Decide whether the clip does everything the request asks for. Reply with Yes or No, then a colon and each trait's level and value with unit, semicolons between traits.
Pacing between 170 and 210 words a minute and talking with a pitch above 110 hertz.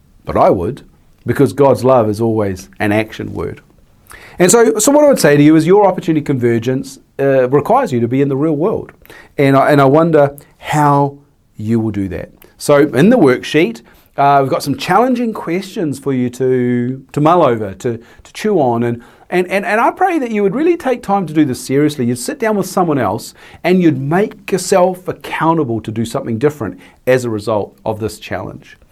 Yes: fast, 205 wpm; medium, 140 Hz